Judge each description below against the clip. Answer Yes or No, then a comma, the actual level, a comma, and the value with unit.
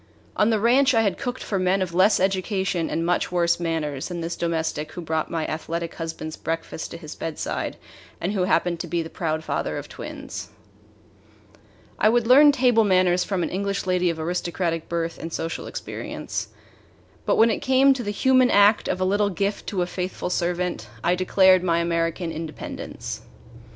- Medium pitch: Yes, medium, 180 Hz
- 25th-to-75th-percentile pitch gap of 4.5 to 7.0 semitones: No, average, 3.3 semitones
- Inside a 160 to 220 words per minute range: Yes, average, 185 wpm